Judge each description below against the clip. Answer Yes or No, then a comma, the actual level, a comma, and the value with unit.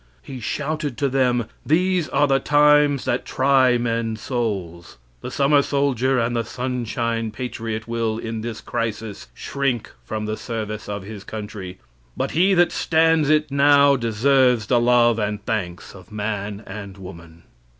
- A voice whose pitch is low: Yes, low, 120 Hz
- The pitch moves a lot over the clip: No, average, 4.5 semitones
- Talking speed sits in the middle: Yes, average, 150 wpm